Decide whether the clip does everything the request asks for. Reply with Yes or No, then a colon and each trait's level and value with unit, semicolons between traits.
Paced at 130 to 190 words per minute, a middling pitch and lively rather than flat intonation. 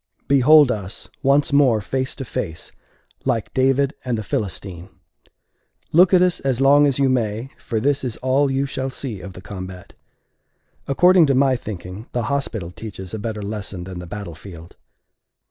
No: average, 170 wpm; low, 120 Hz; wide, 5.7 semitones